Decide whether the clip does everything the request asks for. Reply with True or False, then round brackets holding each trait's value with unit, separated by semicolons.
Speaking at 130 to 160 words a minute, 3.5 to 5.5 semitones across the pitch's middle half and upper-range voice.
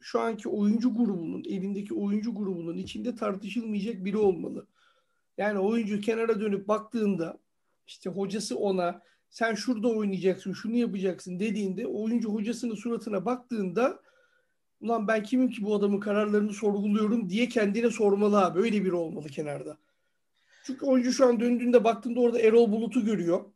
False (140 wpm; 3.1 semitones; 215 Hz)